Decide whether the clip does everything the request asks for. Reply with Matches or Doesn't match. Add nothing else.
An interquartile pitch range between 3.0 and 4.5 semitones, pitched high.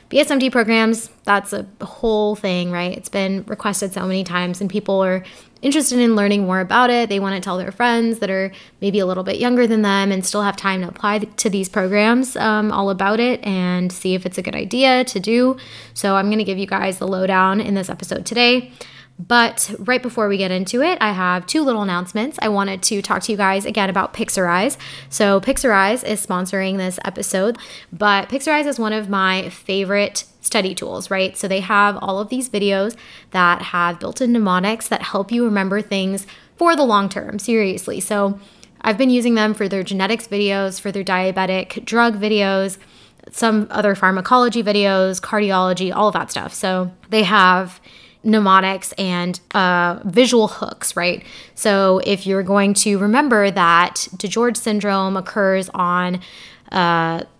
Doesn't match